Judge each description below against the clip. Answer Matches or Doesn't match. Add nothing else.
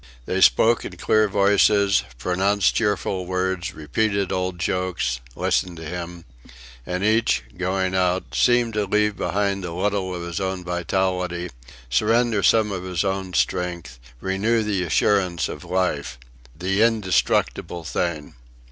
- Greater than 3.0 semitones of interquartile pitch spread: Doesn't match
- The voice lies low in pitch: Matches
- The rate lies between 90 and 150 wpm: Matches